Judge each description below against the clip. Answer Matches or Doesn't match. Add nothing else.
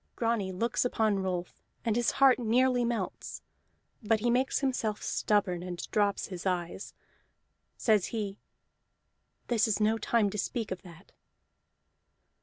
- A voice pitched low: Doesn't match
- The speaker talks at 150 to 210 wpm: Doesn't match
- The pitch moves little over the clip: Doesn't match